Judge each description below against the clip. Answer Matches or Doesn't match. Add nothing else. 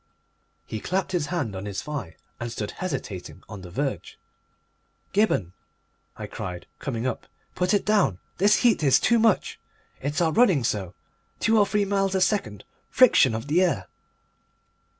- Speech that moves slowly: Doesn't match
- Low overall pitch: Doesn't match